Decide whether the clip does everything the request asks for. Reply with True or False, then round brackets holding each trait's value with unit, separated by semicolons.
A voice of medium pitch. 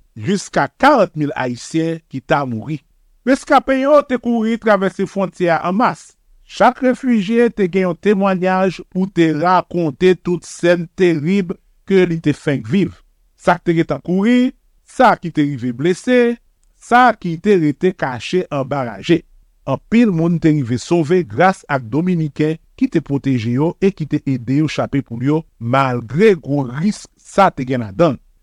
True (170 Hz)